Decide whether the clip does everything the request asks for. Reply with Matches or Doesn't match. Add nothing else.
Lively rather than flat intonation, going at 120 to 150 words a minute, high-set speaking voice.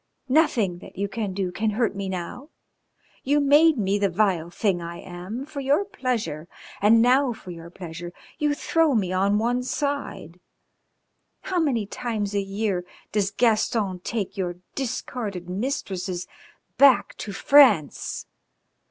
Matches